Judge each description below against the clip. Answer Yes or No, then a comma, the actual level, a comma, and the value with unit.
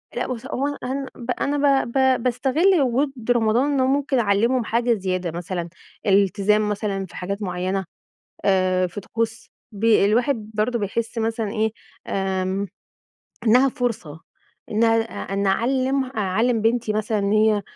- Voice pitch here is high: Yes, high, 220 Hz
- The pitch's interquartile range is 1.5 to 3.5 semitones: No, average, 3.9 semitones